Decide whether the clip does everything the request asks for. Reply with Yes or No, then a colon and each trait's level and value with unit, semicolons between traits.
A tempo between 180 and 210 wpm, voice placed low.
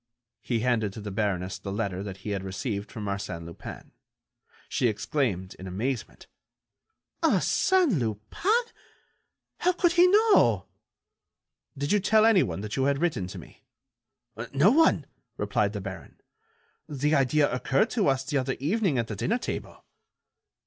No: average, 150 wpm; low, 130 Hz